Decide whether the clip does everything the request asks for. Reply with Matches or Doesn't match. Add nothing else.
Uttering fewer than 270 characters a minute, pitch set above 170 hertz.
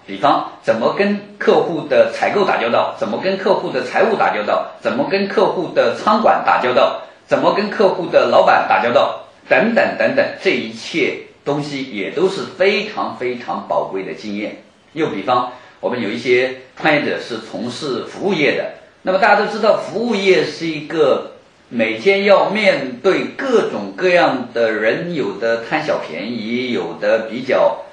Matches